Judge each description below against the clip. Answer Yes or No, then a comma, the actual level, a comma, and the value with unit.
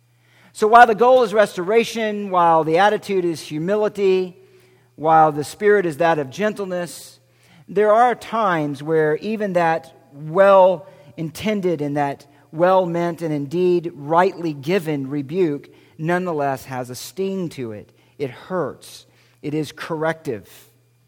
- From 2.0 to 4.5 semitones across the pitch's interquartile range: No, average, 5.0 semitones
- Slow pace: Yes, slow, 130 wpm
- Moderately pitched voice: Yes, medium, 165 Hz